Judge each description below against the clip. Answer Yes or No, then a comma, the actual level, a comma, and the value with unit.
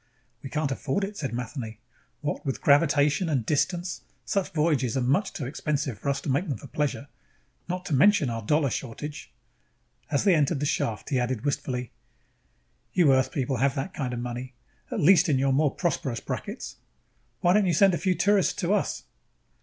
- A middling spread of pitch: Yes, average, 4.7 semitones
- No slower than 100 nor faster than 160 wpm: No, average, 190 wpm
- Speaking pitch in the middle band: Yes, medium, 145 Hz